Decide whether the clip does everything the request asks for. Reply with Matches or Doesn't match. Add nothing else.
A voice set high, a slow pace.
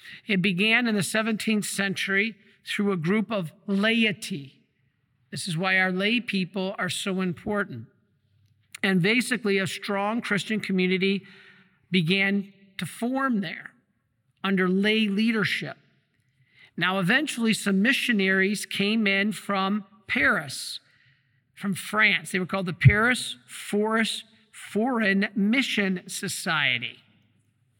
Matches